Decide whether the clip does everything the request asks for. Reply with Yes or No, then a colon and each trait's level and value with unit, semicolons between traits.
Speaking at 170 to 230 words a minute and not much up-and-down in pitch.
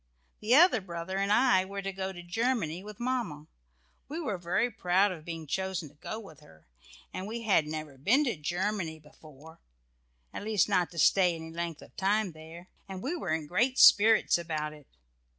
No: average, 190 wpm; average, 4.7 semitones